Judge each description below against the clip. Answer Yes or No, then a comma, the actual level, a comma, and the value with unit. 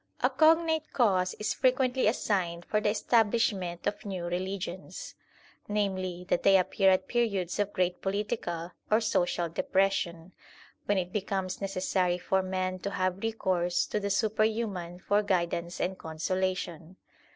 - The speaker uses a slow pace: No, average, 150 wpm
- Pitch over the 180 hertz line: Yes, high, 190 Hz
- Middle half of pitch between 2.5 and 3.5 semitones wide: Yes, average, 2.8 semitones